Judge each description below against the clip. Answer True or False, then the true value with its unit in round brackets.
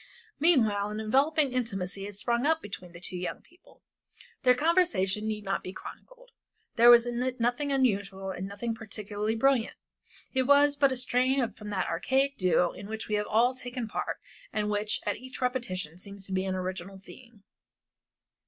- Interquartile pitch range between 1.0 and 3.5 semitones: False (4.7 semitones)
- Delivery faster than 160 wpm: True (170 wpm)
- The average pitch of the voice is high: True (225 Hz)